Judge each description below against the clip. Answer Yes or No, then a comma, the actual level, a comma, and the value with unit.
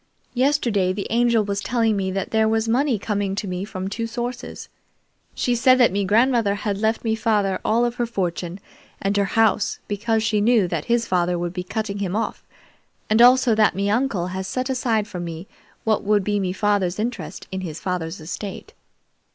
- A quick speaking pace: No, average, 195 wpm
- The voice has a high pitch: Yes, high, 210 Hz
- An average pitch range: Yes, average, 3.3 semitones